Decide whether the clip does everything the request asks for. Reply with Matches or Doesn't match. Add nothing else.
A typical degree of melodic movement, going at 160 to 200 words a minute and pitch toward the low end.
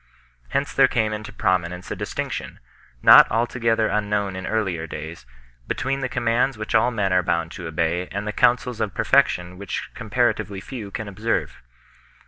Matches